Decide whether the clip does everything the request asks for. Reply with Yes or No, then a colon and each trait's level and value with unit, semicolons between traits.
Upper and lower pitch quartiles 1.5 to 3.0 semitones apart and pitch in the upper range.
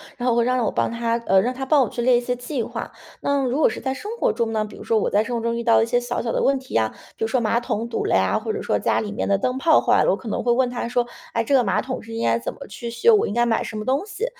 Yes: narrow, 2.4 semitones; high, 240 Hz